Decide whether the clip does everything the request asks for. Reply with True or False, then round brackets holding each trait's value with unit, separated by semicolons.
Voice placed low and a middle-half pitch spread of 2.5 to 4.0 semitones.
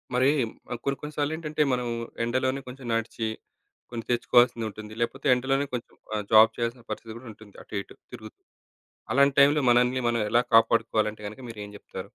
True (120 Hz; 3.0 semitones)